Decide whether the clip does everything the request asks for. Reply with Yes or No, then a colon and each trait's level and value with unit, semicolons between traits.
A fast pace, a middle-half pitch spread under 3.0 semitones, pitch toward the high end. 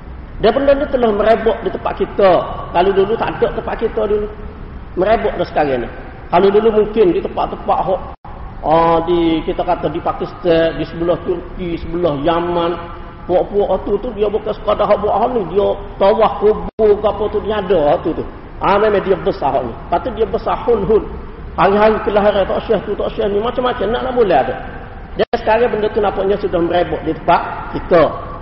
No: fast, 185 wpm; average, 3.9 semitones; high, 205 Hz